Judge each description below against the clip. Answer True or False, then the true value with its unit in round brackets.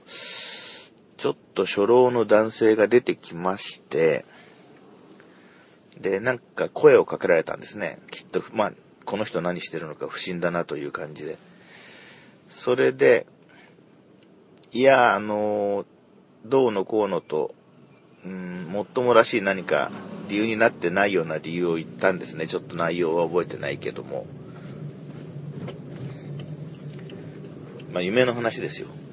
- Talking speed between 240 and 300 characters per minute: True (255 characters per minute)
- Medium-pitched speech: True (150 Hz)